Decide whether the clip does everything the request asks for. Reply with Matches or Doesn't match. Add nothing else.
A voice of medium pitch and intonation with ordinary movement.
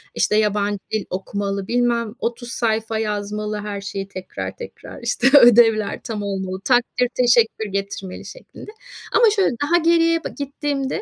Doesn't match